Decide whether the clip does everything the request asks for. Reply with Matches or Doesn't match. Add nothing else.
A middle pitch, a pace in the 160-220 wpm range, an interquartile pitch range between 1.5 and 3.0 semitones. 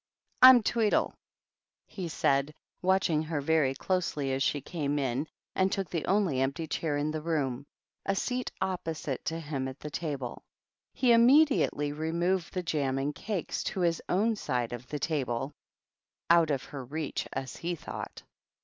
Doesn't match